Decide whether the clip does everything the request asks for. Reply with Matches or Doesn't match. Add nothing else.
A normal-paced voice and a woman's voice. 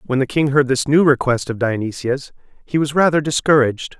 Doesn't match